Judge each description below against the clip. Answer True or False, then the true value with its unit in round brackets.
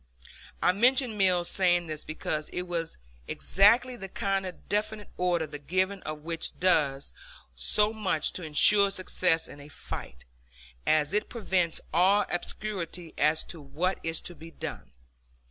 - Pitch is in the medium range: True (180 Hz)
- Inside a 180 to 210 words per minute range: False (150 wpm)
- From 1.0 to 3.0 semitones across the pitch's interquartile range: False (3.9 semitones)